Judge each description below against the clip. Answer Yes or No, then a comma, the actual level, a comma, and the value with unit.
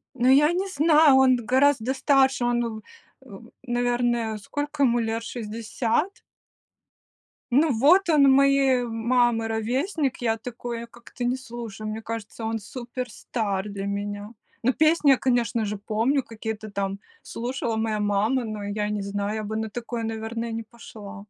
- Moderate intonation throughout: Yes, average, 3.3 semitones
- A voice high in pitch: Yes, high, 235 Hz